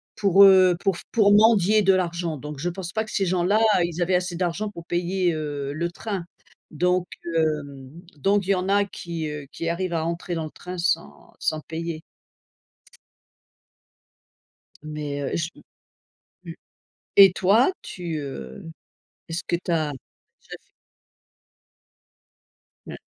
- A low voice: No, medium, 175 Hz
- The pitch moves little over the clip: No, average, 3.1 semitones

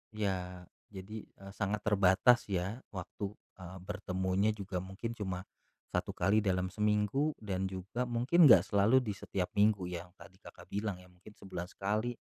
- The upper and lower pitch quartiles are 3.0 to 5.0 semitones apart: No, narrow, 2.6 semitones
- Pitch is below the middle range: Yes, low, 100 Hz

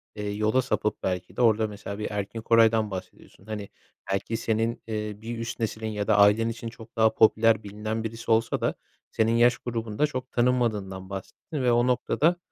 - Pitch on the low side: Yes, low, 110 Hz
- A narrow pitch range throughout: Yes, narrow, 1.8 semitones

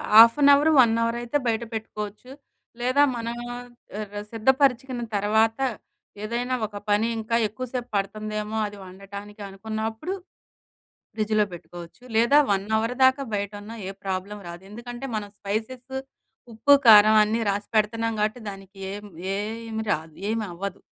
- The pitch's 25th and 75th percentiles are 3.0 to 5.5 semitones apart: No, narrow, 2.5 semitones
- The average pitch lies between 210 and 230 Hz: Yes, high, 220 Hz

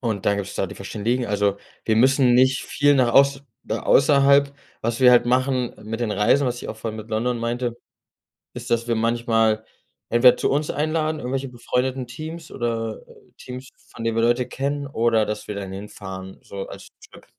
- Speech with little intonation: No, average, 3.1 semitones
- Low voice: Yes, low, 120 Hz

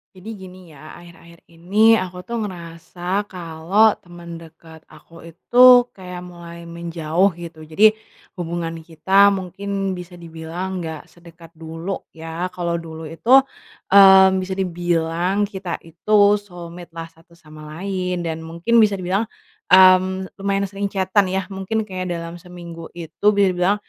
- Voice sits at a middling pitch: Yes, medium, 175 Hz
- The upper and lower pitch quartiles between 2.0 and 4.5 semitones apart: Yes, narrow, 2.5 semitones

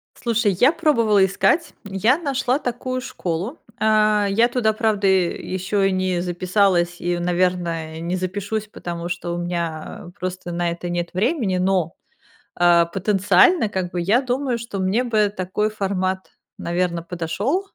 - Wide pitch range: No, average, 3.9 semitones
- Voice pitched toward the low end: No, high, 190 Hz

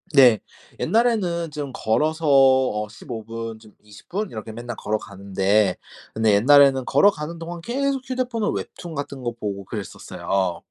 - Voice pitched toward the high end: No, low, 130 Hz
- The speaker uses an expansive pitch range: Yes, wide, 7.5 semitones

